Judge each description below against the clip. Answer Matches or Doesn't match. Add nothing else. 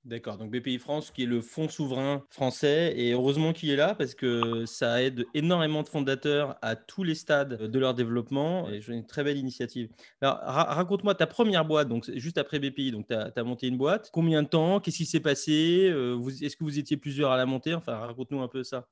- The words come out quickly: Matches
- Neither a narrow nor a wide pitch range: Matches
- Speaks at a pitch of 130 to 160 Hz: Matches